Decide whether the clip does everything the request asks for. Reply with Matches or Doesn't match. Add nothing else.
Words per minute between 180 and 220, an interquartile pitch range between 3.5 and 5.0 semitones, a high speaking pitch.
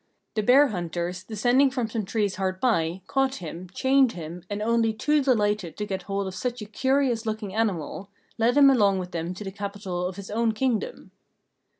Matches